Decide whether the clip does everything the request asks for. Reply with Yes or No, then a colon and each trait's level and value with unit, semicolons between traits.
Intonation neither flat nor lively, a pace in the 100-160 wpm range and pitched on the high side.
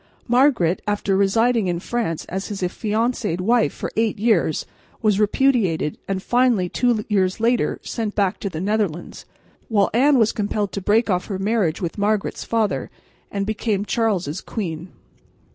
Yes: average, 3.3 semitones; average, 155 wpm; high, 205 Hz